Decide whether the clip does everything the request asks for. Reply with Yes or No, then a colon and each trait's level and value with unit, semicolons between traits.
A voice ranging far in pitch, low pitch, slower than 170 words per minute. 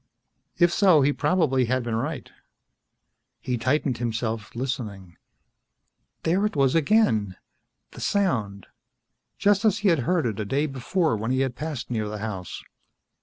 Yes: wide, 6.5 semitones; low, 130 Hz; average, 150 wpm